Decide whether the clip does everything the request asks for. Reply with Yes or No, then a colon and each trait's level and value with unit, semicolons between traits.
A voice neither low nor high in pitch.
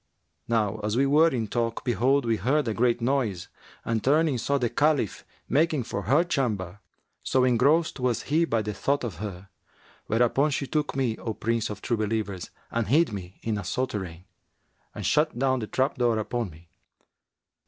No: low, 120 Hz